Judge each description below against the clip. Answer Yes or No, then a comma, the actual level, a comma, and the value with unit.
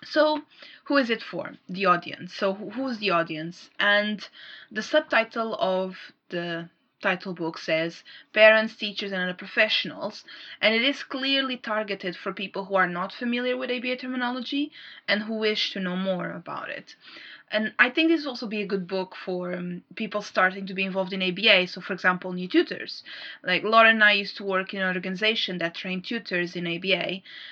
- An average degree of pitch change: Yes, average, 3.7 semitones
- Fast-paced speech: No, average, 185 wpm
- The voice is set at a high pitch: Yes, high, 195 Hz